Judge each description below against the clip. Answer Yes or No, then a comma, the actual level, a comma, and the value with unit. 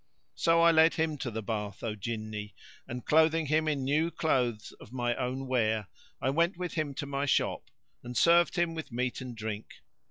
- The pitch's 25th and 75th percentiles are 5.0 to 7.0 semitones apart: Yes, wide, 5.5 semitones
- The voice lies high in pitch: No, low, 130 Hz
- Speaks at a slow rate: No, average, 195 wpm